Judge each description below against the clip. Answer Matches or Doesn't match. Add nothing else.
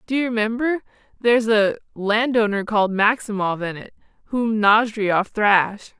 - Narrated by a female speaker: Matches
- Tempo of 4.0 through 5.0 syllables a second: Matches